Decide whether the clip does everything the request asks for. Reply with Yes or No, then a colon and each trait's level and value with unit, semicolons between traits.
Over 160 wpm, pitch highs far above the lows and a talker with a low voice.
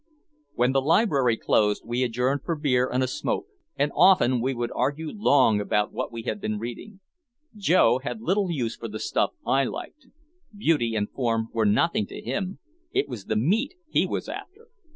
Yes: average, 185 wpm; wide, 6.8 semitones; low, 130 Hz